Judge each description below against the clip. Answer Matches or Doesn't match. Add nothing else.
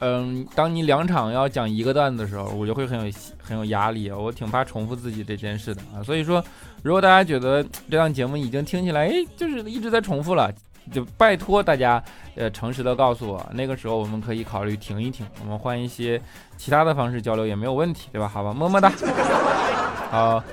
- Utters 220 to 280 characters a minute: Doesn't match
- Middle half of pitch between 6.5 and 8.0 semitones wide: Doesn't match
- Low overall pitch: Matches